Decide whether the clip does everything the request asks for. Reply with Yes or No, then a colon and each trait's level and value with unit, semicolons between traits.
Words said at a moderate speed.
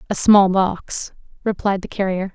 Yes: average, 155 wpm